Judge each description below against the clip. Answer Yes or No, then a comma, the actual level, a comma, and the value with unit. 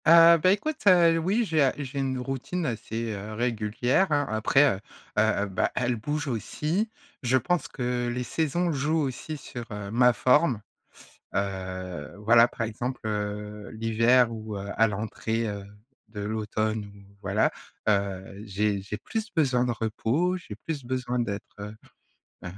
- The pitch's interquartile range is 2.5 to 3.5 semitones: No, wide, 5.4 semitones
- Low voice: Yes, low, 120 Hz